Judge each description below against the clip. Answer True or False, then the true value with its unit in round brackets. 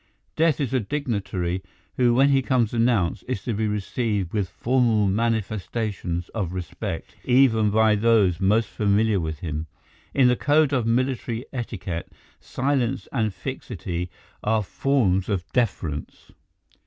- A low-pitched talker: True (110 Hz)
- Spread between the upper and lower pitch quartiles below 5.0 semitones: True (4.5 semitones)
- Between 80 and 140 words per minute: True (135 wpm)